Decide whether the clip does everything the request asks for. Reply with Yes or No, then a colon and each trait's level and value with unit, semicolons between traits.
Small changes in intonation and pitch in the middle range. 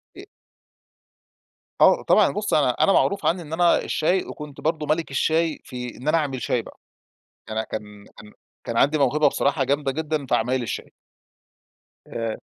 No: average, 4.3 semitones; medium, 145 Hz